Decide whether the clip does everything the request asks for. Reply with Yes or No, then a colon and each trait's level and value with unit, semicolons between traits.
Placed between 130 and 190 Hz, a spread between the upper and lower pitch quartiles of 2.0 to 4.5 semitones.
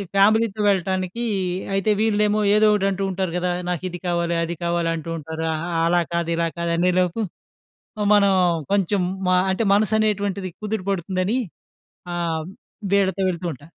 Yes: medium, 185 Hz; average, 2.9 semitones